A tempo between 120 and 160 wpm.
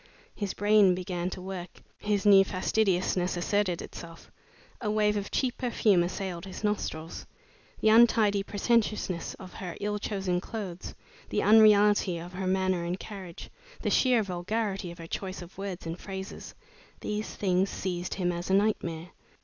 Yes: average, 155 wpm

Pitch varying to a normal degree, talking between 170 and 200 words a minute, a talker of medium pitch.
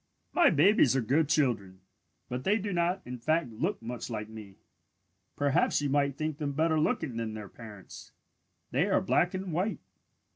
No: wide, 6.6 semitones; average, 175 wpm; medium, 145 Hz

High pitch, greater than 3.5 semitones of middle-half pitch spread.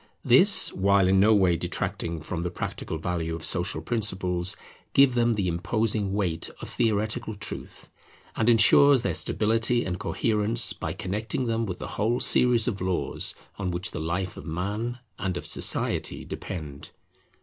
No: low, 100 Hz; average, 4.1 semitones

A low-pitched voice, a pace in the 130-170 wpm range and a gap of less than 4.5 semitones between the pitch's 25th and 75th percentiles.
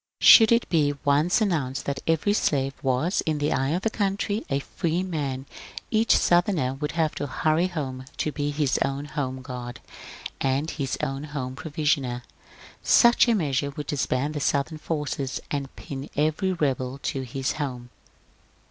No: medium, 145 Hz; average, 165 wpm; average, 3.4 semitones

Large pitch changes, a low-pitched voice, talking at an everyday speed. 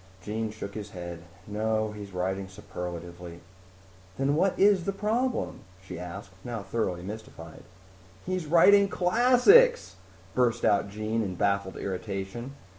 No: wide, 8.9 semitones; low, 105 Hz; slow, 125 wpm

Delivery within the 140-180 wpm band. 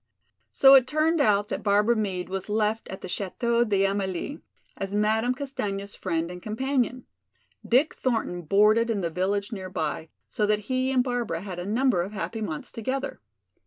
Yes: average, 170 wpm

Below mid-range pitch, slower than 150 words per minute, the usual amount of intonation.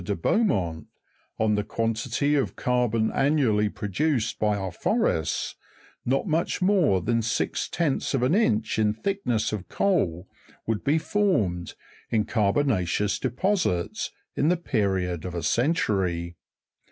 No: low, 110 Hz; slow, 135 wpm; wide, 7.0 semitones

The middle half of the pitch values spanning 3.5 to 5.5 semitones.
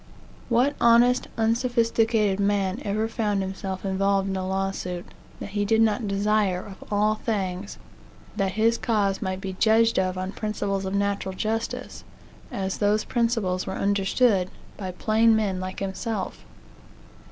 No: average, 2.7 semitones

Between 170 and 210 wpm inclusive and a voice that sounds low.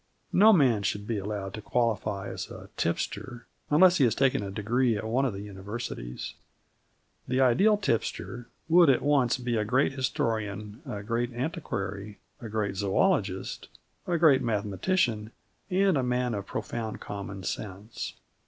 No: average, 155 wpm; low, 115 Hz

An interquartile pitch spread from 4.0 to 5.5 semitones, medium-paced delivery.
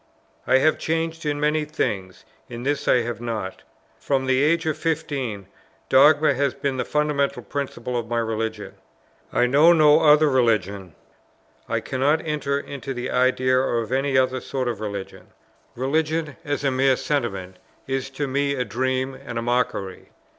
No: average, 3.4 semitones; average, 160 wpm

